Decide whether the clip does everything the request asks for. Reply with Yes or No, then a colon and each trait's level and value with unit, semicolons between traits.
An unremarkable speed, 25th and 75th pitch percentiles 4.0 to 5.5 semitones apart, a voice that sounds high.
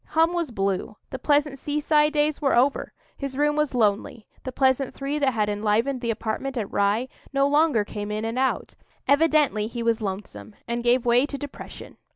Yes: average, 190 wpm; average, 4.9 semitones; very high, 260 Hz